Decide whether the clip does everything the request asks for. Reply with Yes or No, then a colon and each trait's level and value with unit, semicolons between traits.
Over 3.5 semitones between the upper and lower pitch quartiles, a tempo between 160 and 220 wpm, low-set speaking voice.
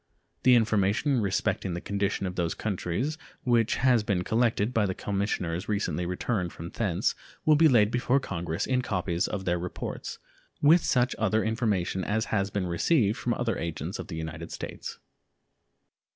Yes: average, 4.9 semitones; average, 165 wpm; low, 105 Hz